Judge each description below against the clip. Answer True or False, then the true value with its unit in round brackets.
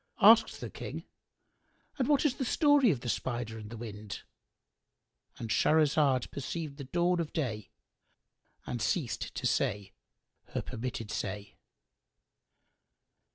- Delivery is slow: True (120 wpm)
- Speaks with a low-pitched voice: True (130 Hz)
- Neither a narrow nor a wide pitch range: False (7.8 semitones)